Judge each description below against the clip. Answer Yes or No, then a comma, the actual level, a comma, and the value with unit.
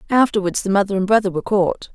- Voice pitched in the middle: No, high, 200 Hz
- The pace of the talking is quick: Yes, fast, 215 wpm